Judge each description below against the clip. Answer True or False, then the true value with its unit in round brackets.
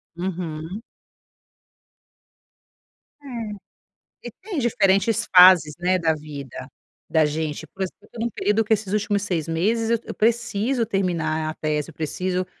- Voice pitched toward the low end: False (185 Hz)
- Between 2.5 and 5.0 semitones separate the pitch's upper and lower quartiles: False (5.5 semitones)